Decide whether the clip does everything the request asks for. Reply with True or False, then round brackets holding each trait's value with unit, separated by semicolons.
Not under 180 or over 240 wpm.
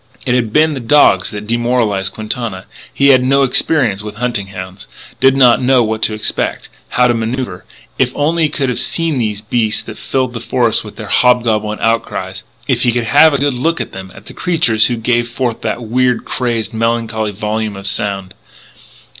True (195 wpm)